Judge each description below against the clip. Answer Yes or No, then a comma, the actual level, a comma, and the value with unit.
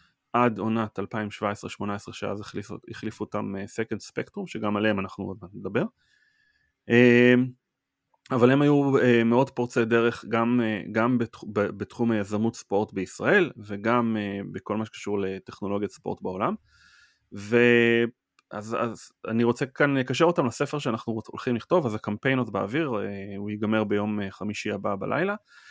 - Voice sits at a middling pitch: No, low, 115 Hz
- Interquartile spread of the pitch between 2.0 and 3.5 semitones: Yes, average, 3.1 semitones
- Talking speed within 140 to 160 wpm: Yes, fast, 150 wpm